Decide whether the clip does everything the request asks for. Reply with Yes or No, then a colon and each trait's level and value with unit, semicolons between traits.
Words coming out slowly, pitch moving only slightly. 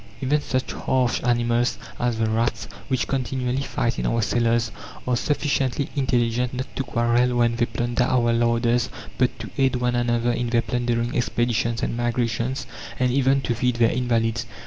No: average, 170 wpm; narrow, 1.3 semitones